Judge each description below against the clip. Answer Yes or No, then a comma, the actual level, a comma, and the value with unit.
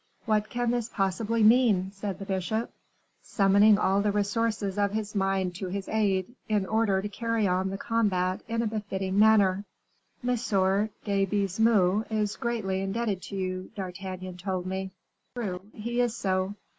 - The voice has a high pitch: Yes, high, 200 Hz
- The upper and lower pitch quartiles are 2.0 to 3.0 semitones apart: Yes, narrow, 2.5 semitones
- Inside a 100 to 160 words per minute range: Yes, average, 155 wpm